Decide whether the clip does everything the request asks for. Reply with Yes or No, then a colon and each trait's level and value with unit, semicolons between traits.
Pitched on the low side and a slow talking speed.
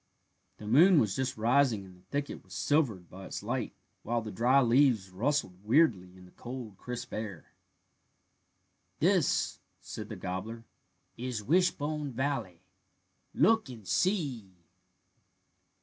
Yes: low, 120 Hz; slow, 130 wpm